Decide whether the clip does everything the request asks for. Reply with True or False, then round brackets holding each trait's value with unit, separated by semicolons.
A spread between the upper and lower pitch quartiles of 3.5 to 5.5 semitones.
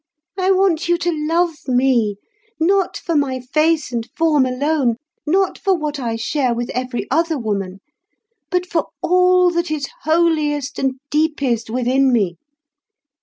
True (5.1 semitones)